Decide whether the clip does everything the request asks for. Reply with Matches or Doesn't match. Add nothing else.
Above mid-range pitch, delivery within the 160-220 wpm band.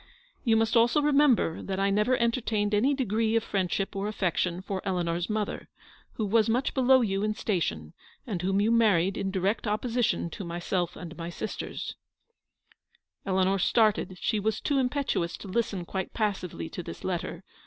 Matches